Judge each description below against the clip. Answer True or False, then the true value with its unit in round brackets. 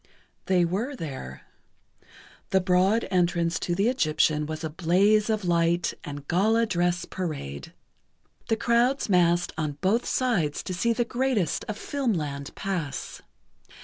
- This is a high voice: False (180 Hz)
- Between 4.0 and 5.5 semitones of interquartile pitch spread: True (5.2 semitones)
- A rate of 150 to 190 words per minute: False (135 wpm)